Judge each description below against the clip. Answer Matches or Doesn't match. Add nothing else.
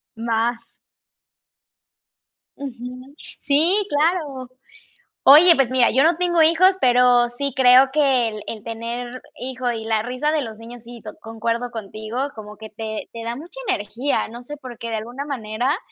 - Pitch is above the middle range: Matches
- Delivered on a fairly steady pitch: Doesn't match